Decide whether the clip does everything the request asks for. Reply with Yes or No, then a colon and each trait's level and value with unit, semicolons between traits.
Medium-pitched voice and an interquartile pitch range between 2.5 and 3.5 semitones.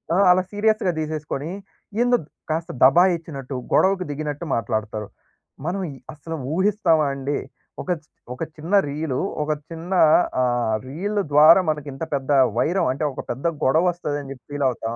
No: medium, 155 Hz; average, 4.3 semitones